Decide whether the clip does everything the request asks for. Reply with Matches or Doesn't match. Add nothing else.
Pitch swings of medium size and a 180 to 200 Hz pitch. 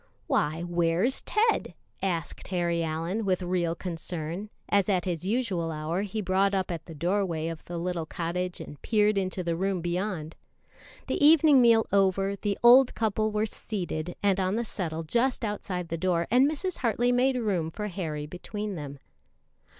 Matches